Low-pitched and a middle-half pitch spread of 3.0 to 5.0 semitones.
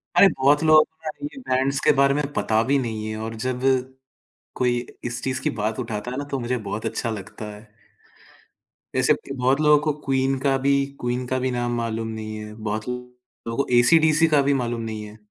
Yes: low, 125 Hz; average, 3.6 semitones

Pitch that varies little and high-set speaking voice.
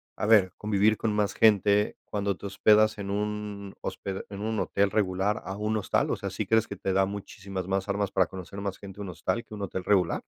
No: narrow, 1.4 semitones; low, 100 Hz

